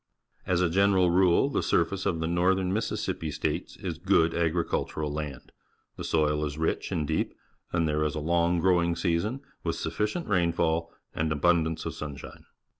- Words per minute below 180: Yes, average, 170 wpm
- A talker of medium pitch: No, very low, 85 Hz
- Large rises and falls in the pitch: No, average, 2.7 semitones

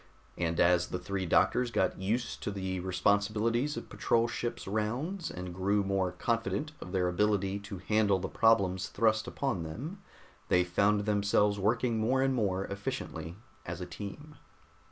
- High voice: No, low, 100 Hz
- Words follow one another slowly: No, average, 160 wpm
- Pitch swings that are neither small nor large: Yes, average, 3.7 semitones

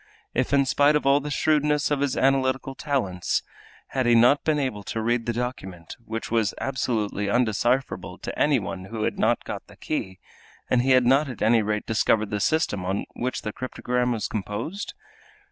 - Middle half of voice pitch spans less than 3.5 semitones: No, average, 4.2 semitones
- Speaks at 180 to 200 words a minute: Yes, average, 185 wpm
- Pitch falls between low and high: No, low, 125 Hz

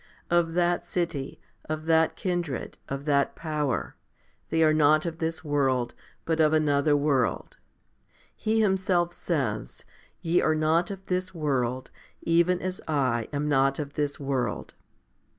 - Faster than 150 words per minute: No, average, 140 wpm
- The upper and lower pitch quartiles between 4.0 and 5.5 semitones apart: No, average, 3.5 semitones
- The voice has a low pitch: No, medium, 155 Hz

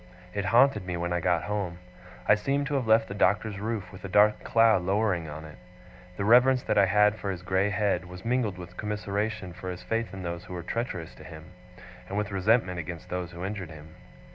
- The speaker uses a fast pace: Yes, fast, 220 wpm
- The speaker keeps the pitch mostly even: No, average, 3.2 semitones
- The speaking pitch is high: No, low, 100 Hz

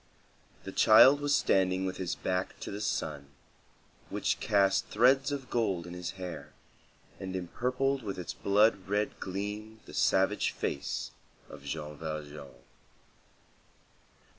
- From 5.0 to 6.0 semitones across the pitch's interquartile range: No, average, 3.8 semitones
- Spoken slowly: Yes, slow, 130 wpm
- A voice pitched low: Yes, very low, 95 Hz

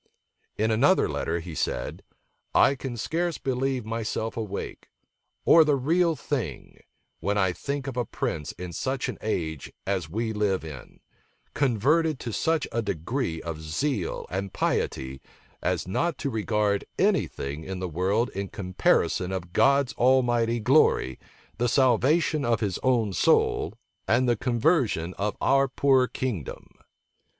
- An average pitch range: No, wide, 6.3 semitones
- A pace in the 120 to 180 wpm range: Yes, average, 145 wpm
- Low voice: Yes, low, 115 Hz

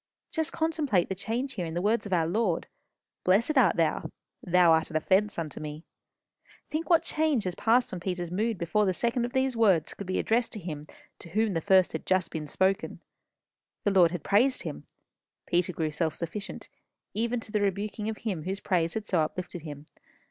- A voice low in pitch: No, high, 190 Hz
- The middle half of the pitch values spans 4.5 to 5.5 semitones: Yes, average, 4.8 semitones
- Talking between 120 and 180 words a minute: No, average, 200 wpm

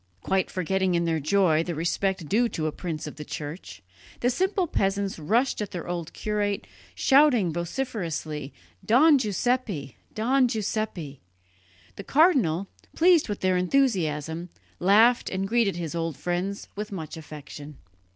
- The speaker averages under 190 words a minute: Yes, average, 140 wpm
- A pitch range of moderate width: No, wide, 5.9 semitones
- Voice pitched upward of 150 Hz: Yes, high, 190 Hz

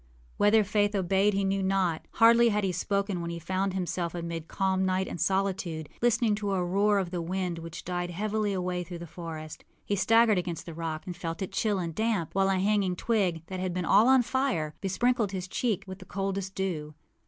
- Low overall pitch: No, high, 190 Hz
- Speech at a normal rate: No, fast, 215 wpm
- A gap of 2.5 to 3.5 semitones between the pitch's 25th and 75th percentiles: Yes, average, 2.8 semitones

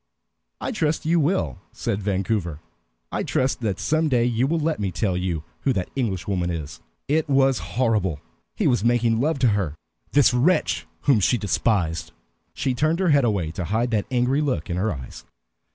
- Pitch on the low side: Yes, low, 115 Hz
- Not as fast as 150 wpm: No, average, 185 wpm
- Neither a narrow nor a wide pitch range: No, wide, 6.6 semitones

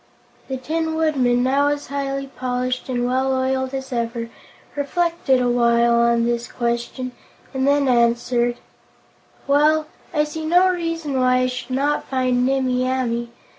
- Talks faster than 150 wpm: No, average, 145 wpm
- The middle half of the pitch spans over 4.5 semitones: No, average, 2.7 semitones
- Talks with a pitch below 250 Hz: No, very high, 260 Hz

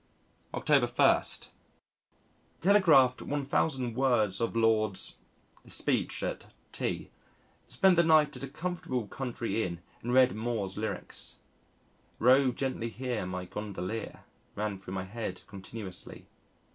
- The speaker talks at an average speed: No, slow, 120 wpm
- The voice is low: Yes, low, 115 Hz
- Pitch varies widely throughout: No, average, 4.2 semitones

